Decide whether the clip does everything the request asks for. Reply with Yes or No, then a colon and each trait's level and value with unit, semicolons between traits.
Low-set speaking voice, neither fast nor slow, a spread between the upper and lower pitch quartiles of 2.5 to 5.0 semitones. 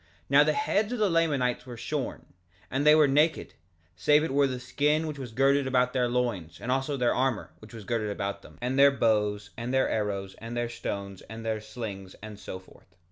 No: low, 125 Hz; fast, 215 wpm; average, 4.7 semitones